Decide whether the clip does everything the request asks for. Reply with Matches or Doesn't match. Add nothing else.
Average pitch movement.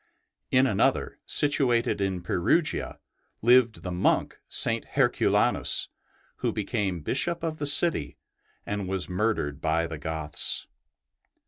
Doesn't match